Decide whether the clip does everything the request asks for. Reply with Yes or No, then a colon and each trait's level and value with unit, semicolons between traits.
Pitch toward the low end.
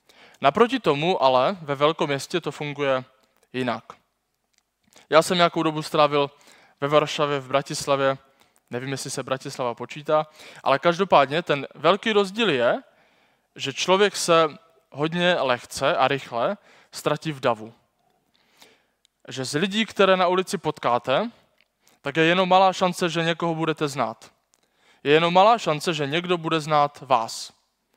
No: medium, 155 Hz